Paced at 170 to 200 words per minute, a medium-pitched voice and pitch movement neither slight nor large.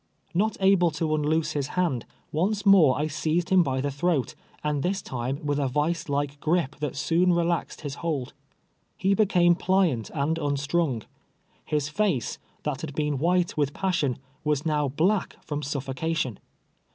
No: average, 155 wpm; medium, 155 Hz; average, 3.5 semitones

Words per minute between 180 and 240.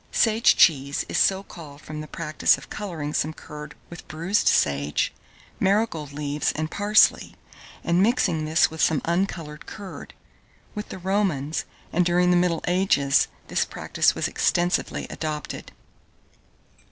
No: average, 140 wpm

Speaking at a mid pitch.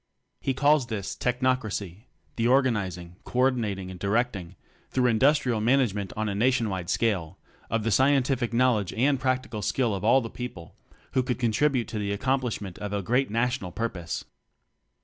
No: low, 115 Hz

